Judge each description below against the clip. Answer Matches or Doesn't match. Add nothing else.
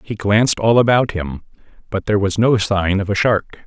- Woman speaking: Doesn't match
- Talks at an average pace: Doesn't match